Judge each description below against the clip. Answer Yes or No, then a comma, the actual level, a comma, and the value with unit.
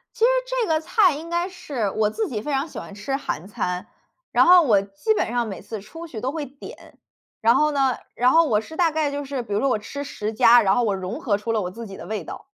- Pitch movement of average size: No, wide, 6.7 semitones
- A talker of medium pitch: No, very high, 250 Hz